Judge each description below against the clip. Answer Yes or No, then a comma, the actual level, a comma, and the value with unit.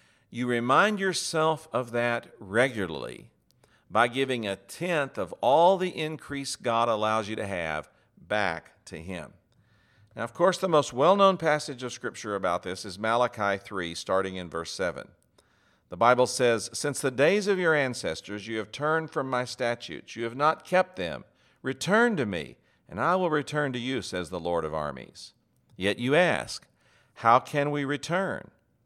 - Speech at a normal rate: Yes, average, 170 wpm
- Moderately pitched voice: No, low, 125 Hz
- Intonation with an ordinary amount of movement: No, wide, 6.2 semitones